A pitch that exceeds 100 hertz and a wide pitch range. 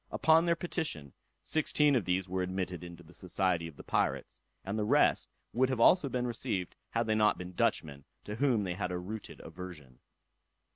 No: very low, 95 Hz; wide, 5.7 semitones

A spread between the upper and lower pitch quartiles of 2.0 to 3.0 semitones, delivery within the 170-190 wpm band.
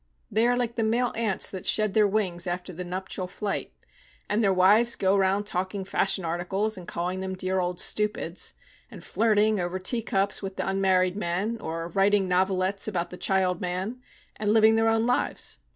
Yes: average, 2.7 semitones; average, 185 wpm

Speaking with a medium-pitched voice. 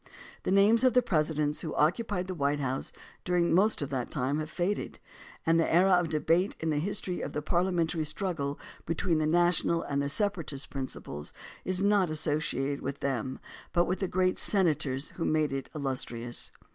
Yes: medium, 160 Hz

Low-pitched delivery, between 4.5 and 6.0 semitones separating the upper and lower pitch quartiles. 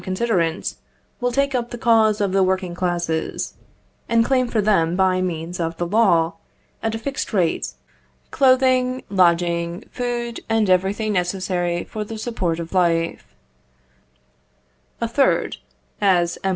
No: high, 190 Hz; average, 4.9 semitones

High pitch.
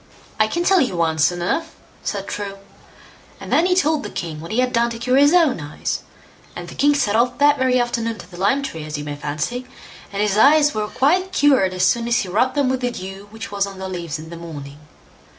Yes: high, 220 Hz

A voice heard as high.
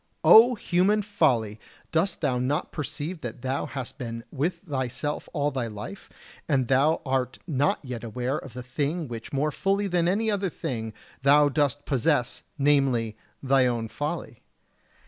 No: medium, 140 Hz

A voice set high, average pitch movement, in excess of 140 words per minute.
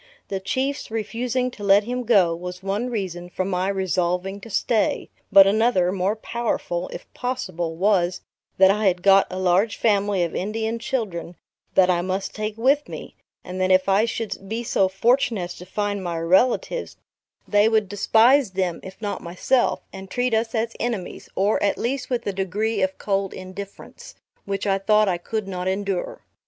Yes: high, 200 Hz; average, 3.3 semitones; average, 180 wpm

